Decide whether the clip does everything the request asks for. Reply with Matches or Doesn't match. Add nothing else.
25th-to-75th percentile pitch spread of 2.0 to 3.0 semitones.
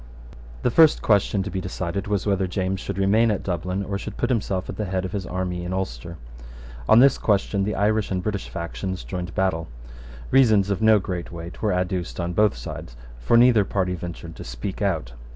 Matches